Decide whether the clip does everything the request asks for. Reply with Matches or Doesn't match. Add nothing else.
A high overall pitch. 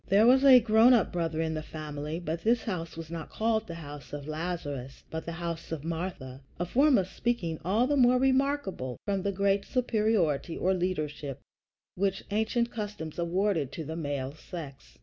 Doesn't match